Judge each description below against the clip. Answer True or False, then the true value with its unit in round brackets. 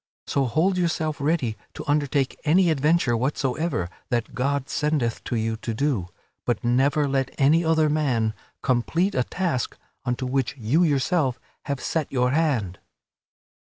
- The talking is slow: False (145 wpm)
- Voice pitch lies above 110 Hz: True (140 Hz)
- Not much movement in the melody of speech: False (4.2 semitones)